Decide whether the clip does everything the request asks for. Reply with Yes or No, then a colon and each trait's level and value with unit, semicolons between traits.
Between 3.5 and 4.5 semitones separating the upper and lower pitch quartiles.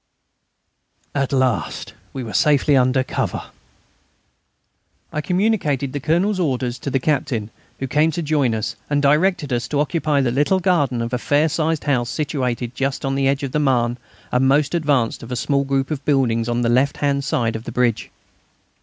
No: average, 3.1 semitones